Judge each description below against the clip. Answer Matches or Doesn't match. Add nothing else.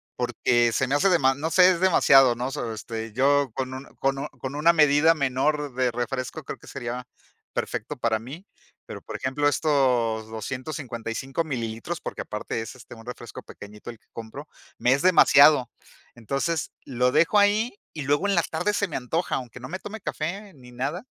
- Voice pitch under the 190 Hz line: Matches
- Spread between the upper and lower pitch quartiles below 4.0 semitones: Doesn't match